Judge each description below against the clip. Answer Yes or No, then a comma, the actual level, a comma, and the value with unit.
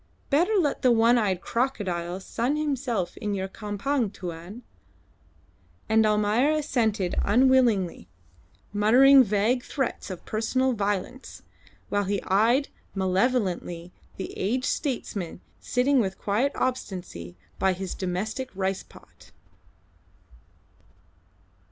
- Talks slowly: Yes, slow, 105 wpm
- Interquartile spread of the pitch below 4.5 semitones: No, average, 5.1 semitones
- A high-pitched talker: Yes, high, 215 Hz